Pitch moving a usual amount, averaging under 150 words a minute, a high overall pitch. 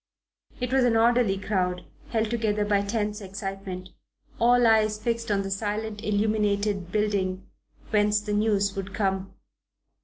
No: narrow, 2.0 semitones; slow, 135 wpm; high, 210 Hz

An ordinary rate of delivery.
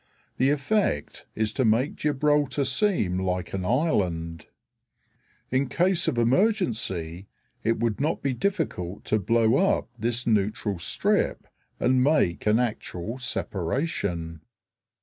No: slow, 120 wpm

